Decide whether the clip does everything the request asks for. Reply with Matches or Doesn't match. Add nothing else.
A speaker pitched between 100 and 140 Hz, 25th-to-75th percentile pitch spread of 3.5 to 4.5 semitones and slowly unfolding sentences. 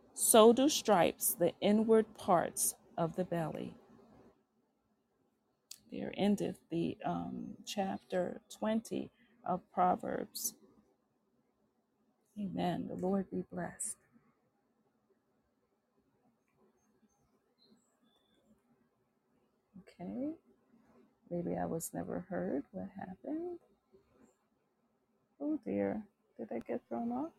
Doesn't match